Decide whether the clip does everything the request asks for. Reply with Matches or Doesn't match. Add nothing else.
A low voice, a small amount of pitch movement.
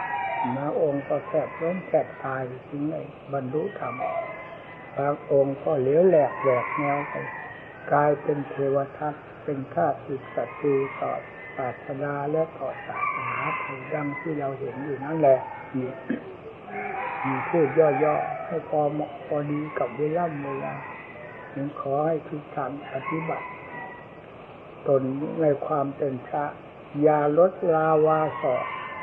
Doesn't match